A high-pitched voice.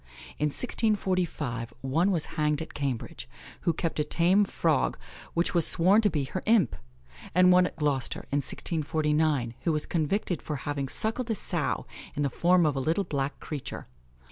No: medium, 160 Hz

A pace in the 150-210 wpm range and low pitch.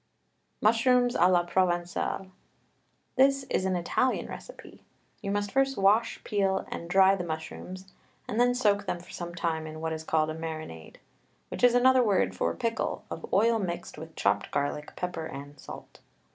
No: average, 170 wpm; medium, 185 Hz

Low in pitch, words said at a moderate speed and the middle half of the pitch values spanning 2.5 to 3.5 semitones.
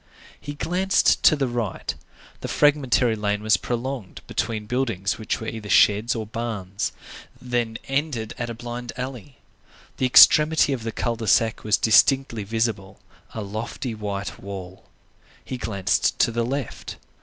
Yes: low, 115 Hz; average, 145 wpm; average, 3.2 semitones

